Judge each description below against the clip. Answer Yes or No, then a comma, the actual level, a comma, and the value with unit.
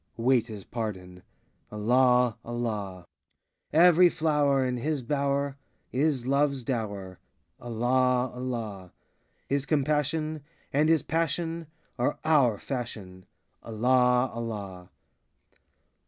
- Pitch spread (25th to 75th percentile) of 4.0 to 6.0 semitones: Yes, average, 4.3 semitones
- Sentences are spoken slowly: Yes, slow, 95 wpm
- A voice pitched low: Yes, low, 125 Hz